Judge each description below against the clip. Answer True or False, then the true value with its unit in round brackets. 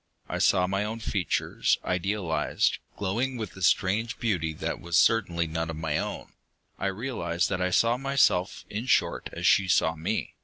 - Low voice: True (95 Hz)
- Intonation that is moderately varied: True (4.7 semitones)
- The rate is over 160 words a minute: True (175 wpm)